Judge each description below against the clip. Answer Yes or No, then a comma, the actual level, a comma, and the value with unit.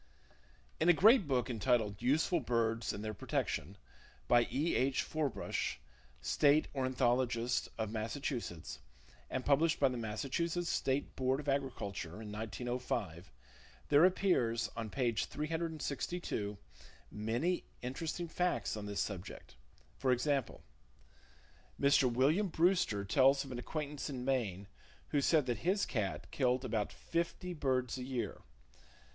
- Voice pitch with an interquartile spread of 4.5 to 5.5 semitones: Yes, average, 4.9 semitones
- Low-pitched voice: Yes, low, 130 Hz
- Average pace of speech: No, slow, 130 wpm